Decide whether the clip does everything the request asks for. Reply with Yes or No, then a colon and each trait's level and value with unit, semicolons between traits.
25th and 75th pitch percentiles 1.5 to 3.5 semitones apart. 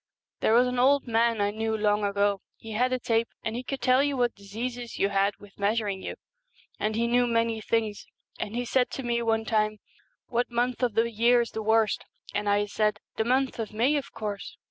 Yes: narrow, 2.5 semitones